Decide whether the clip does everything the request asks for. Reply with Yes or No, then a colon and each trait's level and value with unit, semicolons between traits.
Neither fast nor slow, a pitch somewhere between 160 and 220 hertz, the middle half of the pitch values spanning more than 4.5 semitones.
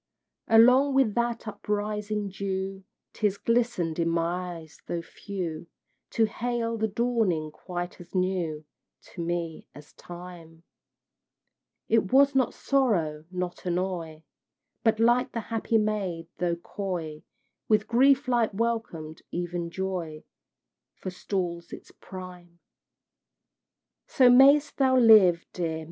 No: slow, 115 wpm; high, 190 Hz; average, 5.0 semitones